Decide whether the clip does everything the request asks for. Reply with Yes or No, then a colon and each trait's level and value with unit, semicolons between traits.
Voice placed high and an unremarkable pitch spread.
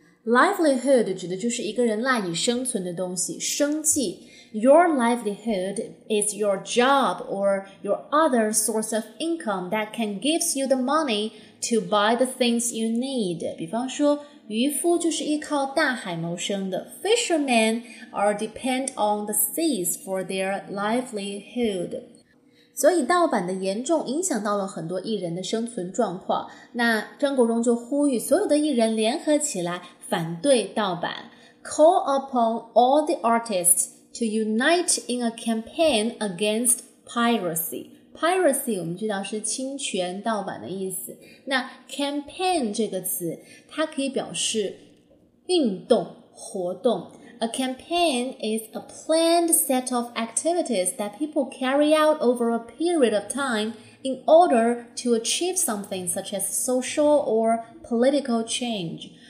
Yes: high, 235 Hz; average, 5.0 semitones